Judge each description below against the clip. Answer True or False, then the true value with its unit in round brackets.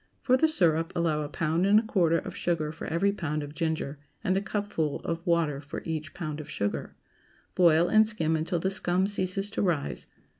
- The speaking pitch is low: False (170 Hz)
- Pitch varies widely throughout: False (3.6 semitones)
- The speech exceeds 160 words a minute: True (200 wpm)